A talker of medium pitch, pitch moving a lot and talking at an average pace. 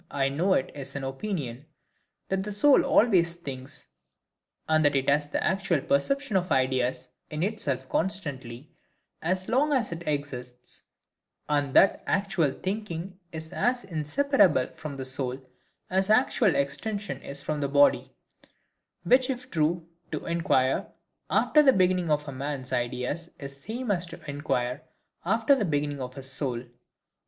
Yes: medium, 155 Hz; wide, 6.0 semitones; average, 150 wpm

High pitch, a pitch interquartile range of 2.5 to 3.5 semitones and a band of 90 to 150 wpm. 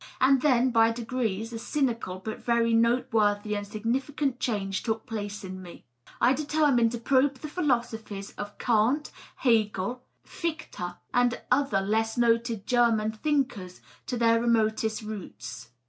Yes: high, 230 Hz; average, 3.1 semitones; average, 140 wpm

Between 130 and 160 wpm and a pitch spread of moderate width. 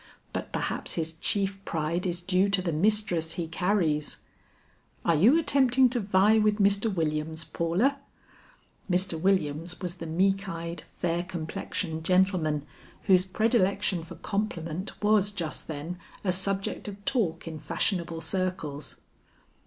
Yes: slow, 135 wpm; average, 3.4 semitones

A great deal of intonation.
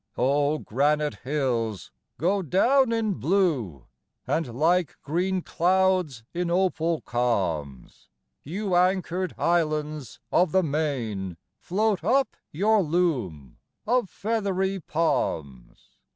Yes: wide, 6.4 semitones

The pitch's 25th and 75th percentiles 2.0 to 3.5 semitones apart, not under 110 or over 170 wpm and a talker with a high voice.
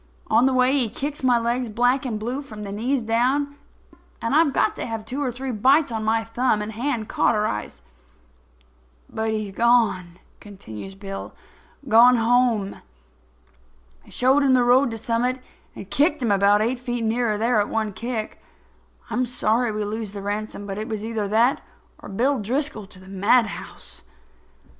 Yes: average, 3.1 semitones; average, 165 wpm; high, 230 Hz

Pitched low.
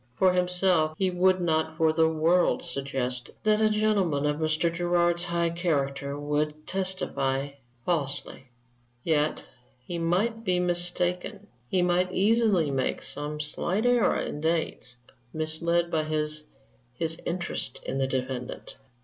No: medium, 165 Hz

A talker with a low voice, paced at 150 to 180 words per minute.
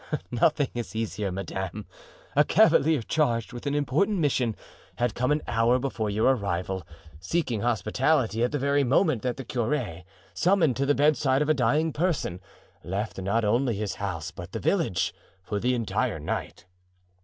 Yes: low, 120 Hz; average, 165 wpm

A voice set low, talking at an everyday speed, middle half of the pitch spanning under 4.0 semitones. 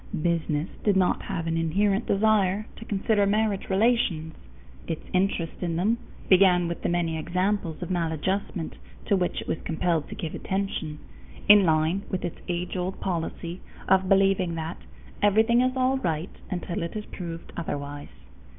No: medium, 180 Hz; average, 160 wpm; average, 3.2 semitones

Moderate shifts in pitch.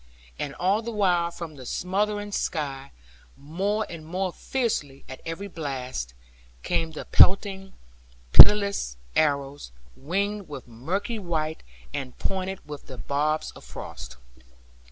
No: wide, 5.9 semitones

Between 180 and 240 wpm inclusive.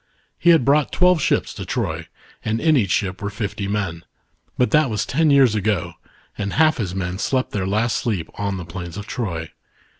Yes: average, 200 wpm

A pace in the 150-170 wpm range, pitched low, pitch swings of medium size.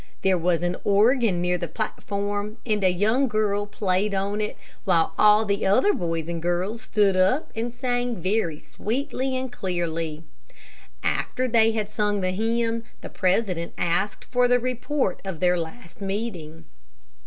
No: average, 155 wpm; high, 205 Hz; average, 4.2 semitones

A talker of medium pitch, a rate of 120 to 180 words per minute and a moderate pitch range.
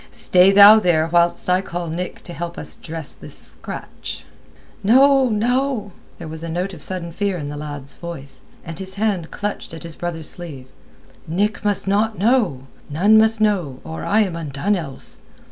Yes: medium, 180 Hz; average, 175 wpm; average, 4.3 semitones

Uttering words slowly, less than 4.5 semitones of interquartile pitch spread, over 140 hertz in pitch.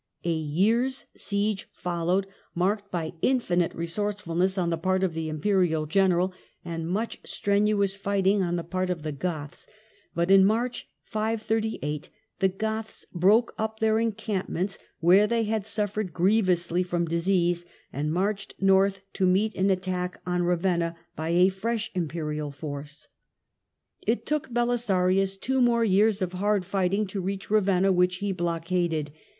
No: average, 145 wpm; average, 3.3 semitones; high, 190 Hz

